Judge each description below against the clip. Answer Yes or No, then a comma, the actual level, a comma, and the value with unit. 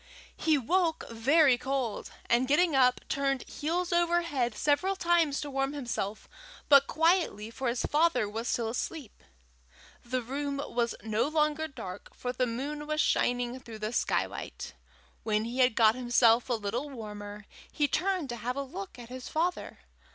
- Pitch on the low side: No, very high, 260 Hz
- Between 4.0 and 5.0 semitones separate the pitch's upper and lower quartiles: Yes, average, 4.4 semitones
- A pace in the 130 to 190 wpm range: Yes, average, 165 wpm